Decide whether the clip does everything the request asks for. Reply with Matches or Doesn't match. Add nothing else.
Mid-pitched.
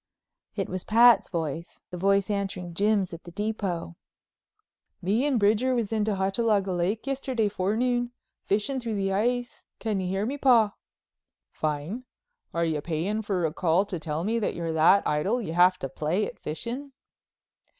Doesn't match